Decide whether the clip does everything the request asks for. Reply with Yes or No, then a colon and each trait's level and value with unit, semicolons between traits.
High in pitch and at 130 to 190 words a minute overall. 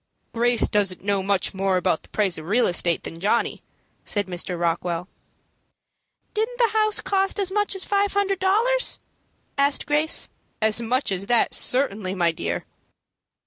Yes: high, 225 Hz; average, 155 wpm